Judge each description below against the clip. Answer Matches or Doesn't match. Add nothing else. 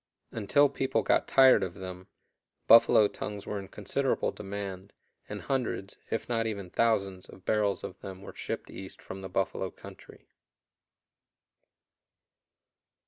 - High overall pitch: Doesn't match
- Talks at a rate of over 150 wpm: Doesn't match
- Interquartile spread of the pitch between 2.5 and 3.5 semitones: Matches